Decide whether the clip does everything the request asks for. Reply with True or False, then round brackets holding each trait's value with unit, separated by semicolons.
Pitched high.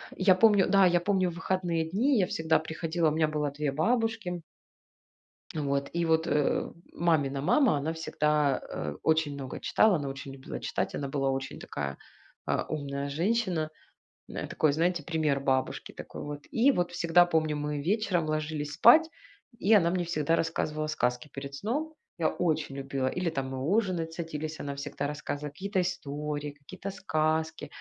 False (155 Hz)